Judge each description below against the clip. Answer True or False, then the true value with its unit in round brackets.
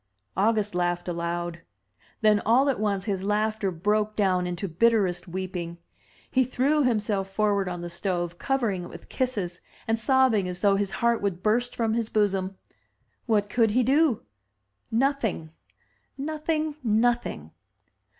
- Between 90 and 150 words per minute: True (145 wpm)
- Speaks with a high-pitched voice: True (210 Hz)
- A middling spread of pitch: True (4.4 semitones)